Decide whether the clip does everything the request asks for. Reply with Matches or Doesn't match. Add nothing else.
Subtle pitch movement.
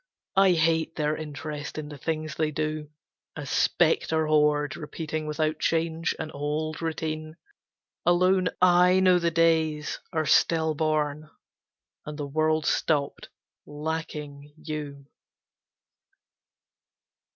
Matches